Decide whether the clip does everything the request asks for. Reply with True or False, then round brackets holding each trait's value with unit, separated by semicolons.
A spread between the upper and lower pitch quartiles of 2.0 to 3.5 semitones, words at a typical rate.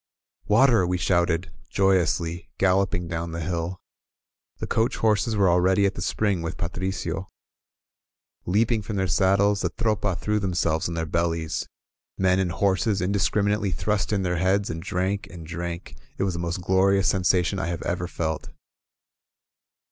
True (2.6 semitones; 165 wpm)